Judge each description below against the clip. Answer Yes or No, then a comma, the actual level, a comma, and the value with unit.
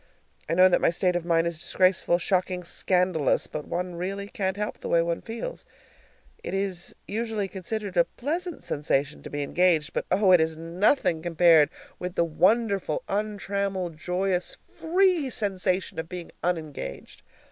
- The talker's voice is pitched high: No, medium, 180 Hz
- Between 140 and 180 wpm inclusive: Yes, average, 160 wpm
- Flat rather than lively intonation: No, average, 3.0 semitones